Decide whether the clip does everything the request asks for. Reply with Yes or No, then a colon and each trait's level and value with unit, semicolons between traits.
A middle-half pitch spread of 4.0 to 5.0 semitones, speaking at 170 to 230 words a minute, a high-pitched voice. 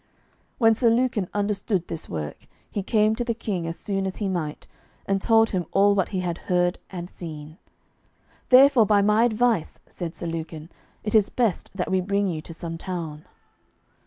Yes: average, 4.3 semitones; average, 185 wpm; high, 195 Hz